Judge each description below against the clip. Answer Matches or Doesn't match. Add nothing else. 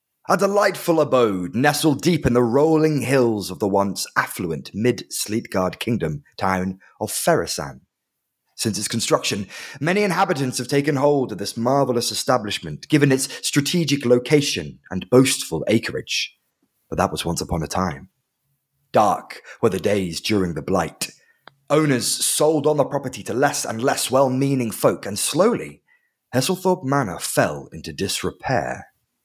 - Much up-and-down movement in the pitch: Matches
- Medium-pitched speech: Doesn't match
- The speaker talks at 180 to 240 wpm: Doesn't match